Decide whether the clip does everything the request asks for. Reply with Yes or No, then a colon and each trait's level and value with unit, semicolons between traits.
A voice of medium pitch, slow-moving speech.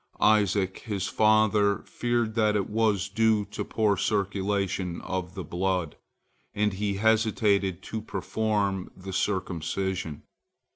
No: low, 100 Hz; slow, 115 wpm